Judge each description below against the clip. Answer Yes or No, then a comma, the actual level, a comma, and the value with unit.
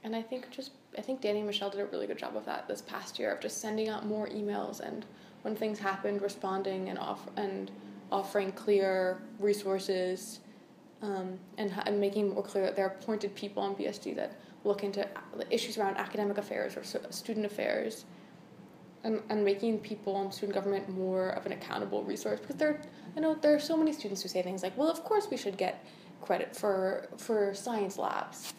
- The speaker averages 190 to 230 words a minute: Yes, average, 200 wpm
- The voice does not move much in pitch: Yes, narrow, 2.2 semitones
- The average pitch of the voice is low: No, high, 205 Hz